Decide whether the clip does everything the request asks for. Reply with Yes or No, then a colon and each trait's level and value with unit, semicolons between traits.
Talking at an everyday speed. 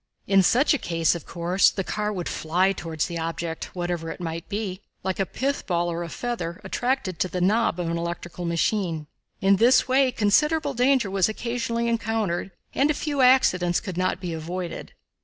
Yes: average, 190 wpm